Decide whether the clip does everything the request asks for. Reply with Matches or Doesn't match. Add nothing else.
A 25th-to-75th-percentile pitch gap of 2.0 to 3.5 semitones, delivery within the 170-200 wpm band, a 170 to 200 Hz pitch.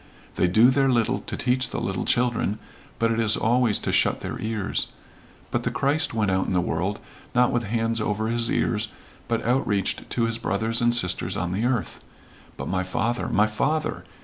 Doesn't match